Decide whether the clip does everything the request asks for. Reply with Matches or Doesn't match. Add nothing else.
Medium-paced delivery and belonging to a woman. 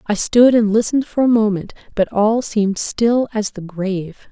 Matches